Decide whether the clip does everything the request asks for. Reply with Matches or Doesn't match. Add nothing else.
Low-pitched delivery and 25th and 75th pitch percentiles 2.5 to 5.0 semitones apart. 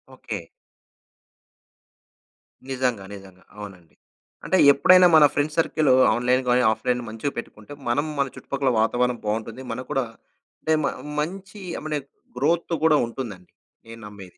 Doesn't match